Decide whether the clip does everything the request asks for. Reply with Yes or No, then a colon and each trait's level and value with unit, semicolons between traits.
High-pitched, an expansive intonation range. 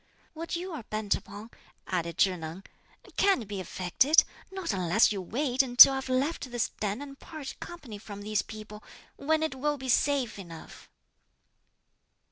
Yes: high, 240 Hz; wide, 6.0 semitones